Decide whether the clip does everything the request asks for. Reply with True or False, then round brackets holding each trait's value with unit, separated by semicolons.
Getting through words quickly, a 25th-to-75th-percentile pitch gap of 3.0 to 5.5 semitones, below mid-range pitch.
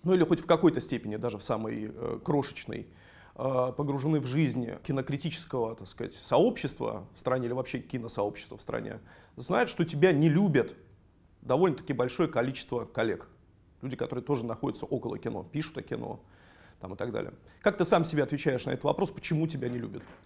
True (180 wpm; 5.2 semitones; 130 Hz)